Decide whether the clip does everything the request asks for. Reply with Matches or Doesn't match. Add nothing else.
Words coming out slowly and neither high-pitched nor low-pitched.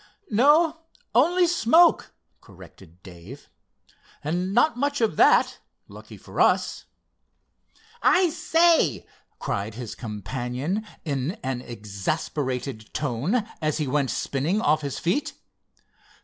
Matches